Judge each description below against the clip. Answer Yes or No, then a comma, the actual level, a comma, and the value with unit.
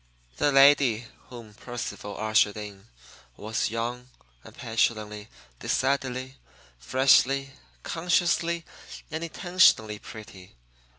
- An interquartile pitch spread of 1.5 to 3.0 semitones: No, average, 4.3 semitones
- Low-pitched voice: Yes, low, 120 Hz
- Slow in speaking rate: Yes, slow, 85 wpm